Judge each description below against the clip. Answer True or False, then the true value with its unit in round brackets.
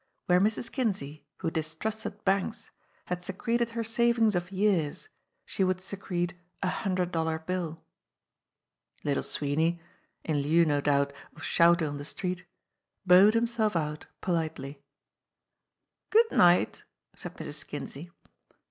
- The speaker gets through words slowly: True (125 wpm)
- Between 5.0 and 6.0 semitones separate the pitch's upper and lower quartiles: False (4.5 semitones)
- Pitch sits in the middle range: True (180 Hz)